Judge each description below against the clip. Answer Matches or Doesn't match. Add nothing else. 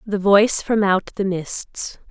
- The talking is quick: Doesn't match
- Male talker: Doesn't match